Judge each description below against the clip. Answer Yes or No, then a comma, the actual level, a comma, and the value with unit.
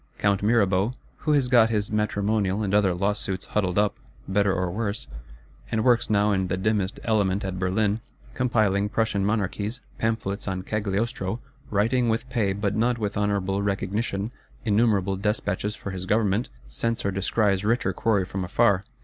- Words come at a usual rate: Yes, average, 155 wpm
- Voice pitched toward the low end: Yes, low, 100 Hz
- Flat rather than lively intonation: Yes, narrow, 2.2 semitones